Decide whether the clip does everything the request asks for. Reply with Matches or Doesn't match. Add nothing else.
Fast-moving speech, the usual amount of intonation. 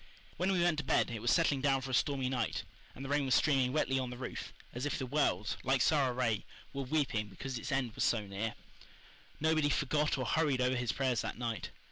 Matches